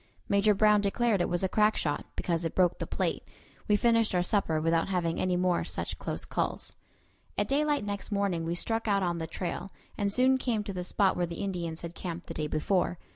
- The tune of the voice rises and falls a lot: No, average, 3.4 semitones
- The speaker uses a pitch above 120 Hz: Yes, high, 190 Hz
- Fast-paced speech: Yes, fast, 220 wpm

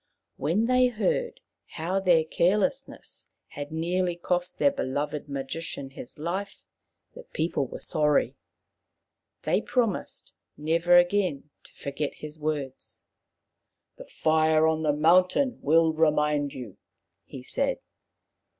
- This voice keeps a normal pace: No, slow, 120 wpm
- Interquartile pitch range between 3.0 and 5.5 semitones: Yes, average, 3.7 semitones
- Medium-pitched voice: Yes, medium, 160 Hz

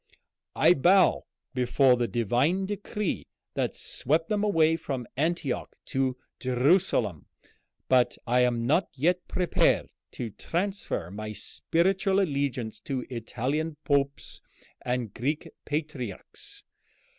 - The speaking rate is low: Yes, slow, 110 wpm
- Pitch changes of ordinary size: No, wide, 6.0 semitones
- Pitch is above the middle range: No, medium, 140 Hz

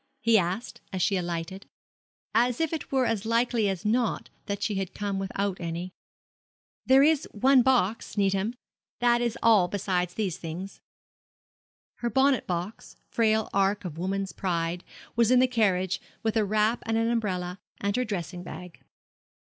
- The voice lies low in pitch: No, high, 205 Hz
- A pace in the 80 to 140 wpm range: No, average, 160 wpm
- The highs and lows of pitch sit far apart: No, average, 4.0 semitones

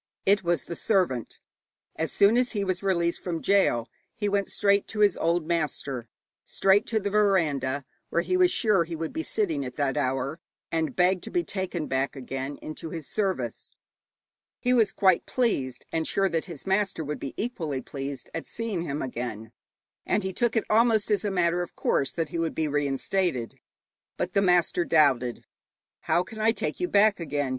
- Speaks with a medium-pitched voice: Yes, medium, 170 Hz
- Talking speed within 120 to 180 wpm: No, average, 190 wpm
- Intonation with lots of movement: Yes, wide, 5.9 semitones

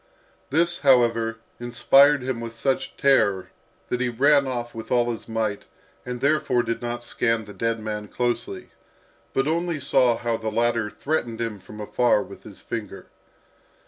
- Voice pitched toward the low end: Yes, low, 120 Hz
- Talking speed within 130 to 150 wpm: No, average, 160 wpm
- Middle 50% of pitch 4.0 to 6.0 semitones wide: No, average, 2.8 semitones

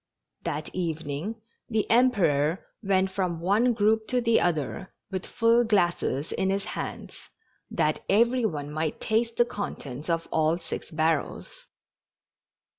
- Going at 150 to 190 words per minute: No, slow, 135 wpm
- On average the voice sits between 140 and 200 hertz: Yes, high, 190 Hz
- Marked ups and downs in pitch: Yes, wide, 5.9 semitones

